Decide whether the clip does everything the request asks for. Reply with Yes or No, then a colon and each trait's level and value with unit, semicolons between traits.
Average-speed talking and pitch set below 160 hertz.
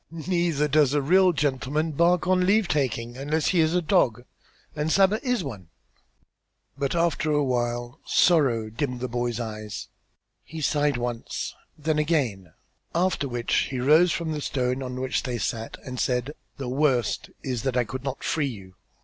Yes: average, 170 wpm; medium, 140 Hz